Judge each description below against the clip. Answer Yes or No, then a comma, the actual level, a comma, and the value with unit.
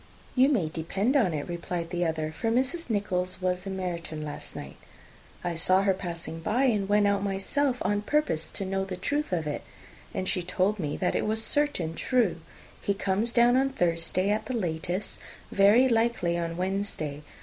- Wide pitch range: No, average, 4.6 semitones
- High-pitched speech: Yes, high, 195 Hz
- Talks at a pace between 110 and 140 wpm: No, average, 185 wpm